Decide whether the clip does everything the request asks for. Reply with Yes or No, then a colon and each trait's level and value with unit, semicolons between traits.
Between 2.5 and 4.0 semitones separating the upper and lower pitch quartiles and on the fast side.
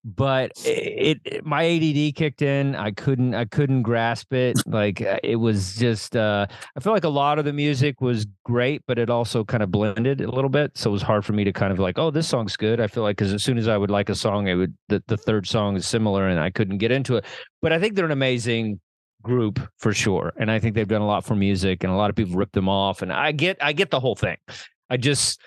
No: average, 4.8 semitones; fast, 265 wpm